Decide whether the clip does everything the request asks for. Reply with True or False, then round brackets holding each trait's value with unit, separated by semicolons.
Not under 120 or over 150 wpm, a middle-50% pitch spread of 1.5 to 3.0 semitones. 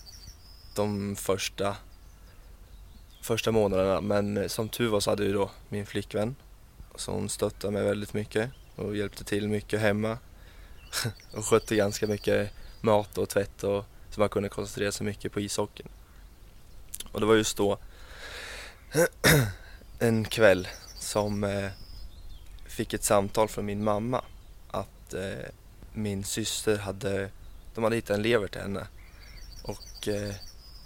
True (130 wpm; 2.4 semitones)